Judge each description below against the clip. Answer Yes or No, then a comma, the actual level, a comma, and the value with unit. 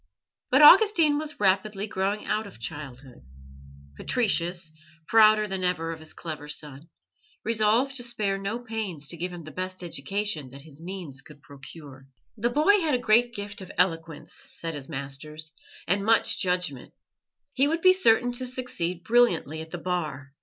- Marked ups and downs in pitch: Yes, wide, 6.3 semitones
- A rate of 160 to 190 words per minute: Yes, average, 165 wpm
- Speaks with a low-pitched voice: No, medium, 185 Hz